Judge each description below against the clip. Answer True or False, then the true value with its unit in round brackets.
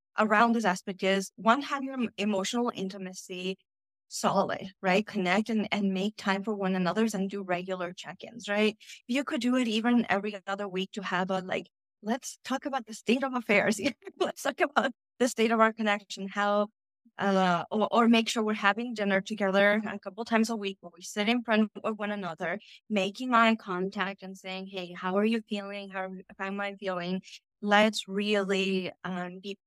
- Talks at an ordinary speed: True (195 wpm)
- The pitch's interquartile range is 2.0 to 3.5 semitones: True (2.7 semitones)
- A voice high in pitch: True (205 Hz)